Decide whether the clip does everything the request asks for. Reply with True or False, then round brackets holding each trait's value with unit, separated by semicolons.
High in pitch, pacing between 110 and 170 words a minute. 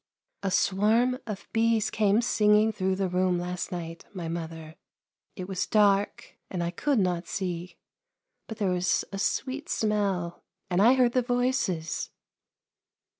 True (195 Hz; 150 wpm)